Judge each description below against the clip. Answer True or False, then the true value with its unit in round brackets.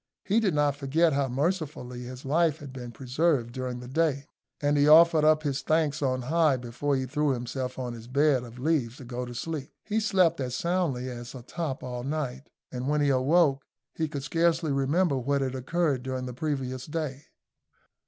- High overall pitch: False (140 Hz)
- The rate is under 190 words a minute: False (195 wpm)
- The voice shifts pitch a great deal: False (3.6 semitones)